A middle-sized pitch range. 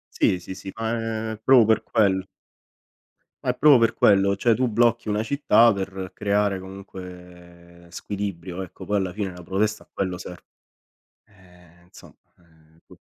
Yes: average, 3.6 semitones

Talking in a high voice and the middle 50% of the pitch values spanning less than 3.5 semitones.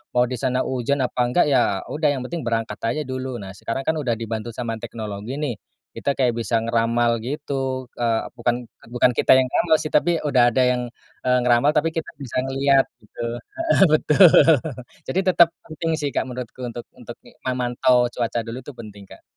No: low, 125 Hz; average, 3.0 semitones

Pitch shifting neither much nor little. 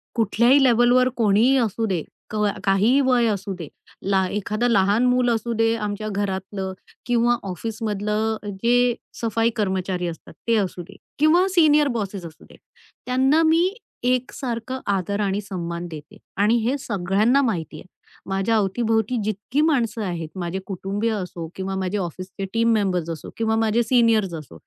Yes: average, 3.8 semitones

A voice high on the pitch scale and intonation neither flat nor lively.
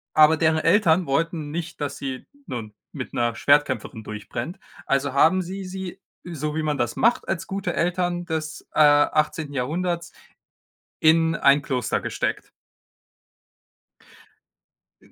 No: medium, 155 Hz; average, 3.7 semitones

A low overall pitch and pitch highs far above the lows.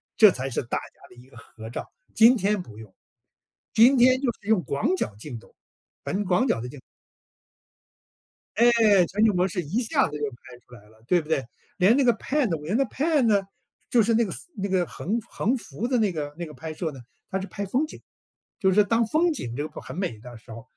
No: medium, 185 Hz; wide, 9.0 semitones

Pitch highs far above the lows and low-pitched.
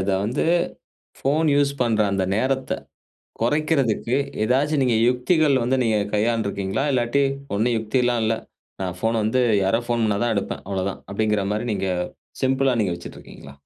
No: average, 3.9 semitones; low, 115 Hz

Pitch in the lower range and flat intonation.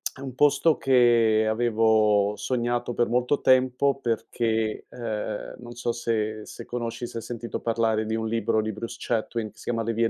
Yes: low, 115 Hz; narrow, 1.8 semitones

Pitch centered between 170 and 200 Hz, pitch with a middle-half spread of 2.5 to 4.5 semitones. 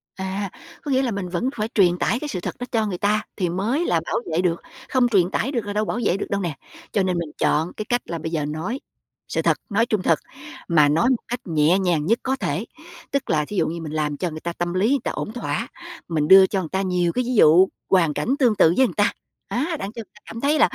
No: high, 190 Hz; wide, 5.4 semitones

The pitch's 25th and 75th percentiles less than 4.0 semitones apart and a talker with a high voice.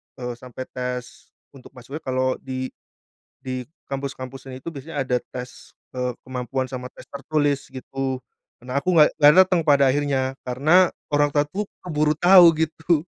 No: average, 2.7 semitones; low, 135 Hz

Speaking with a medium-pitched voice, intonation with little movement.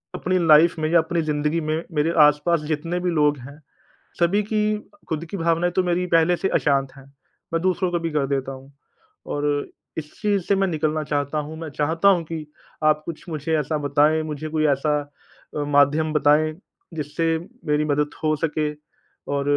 Yes: medium, 155 Hz; narrow, 2.1 semitones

